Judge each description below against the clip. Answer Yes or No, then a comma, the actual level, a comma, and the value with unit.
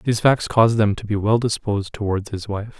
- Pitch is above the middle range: No, low, 110 Hz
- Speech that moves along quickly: Yes, fast, 235 wpm